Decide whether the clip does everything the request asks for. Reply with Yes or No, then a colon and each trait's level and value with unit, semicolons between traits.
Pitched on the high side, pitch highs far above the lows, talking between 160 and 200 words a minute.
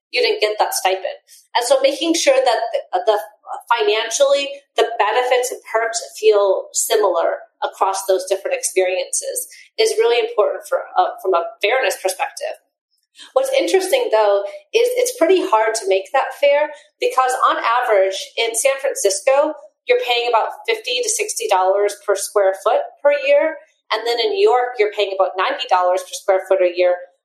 Yes: very high, 255 Hz; wide, 7.5 semitones; average, 165 wpm